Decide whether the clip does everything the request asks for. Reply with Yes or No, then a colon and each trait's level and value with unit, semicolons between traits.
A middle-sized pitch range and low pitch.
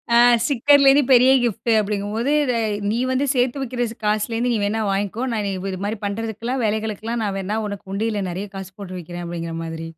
No: average, 3.3 semitones; high, 215 Hz